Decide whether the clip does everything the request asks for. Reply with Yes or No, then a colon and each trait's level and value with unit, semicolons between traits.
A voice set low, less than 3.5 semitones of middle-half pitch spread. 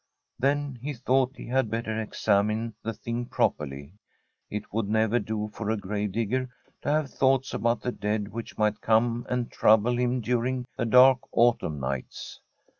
Yes: low, 115 Hz; average, 2.8 semitones